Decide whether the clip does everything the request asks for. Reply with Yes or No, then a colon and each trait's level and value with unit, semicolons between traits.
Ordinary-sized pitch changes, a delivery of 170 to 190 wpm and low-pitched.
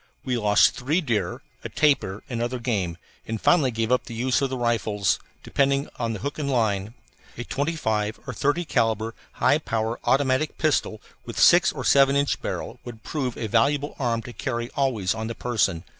Yes: average, 3.8 semitones; average, 185 wpm; low, 120 Hz